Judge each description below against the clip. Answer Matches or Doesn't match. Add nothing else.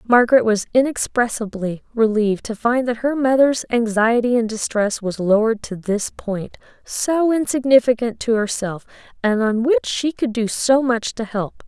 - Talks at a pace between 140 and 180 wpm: Matches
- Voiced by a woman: Matches